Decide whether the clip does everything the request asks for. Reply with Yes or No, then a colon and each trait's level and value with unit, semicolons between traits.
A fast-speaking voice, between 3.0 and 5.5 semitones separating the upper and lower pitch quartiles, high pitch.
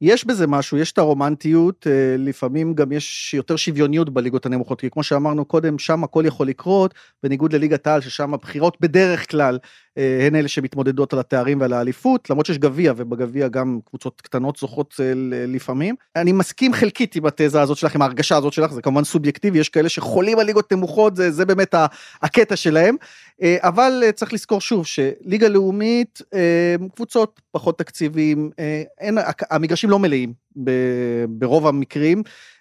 No: fast, 155 wpm; average, 4.7 semitones; medium, 155 Hz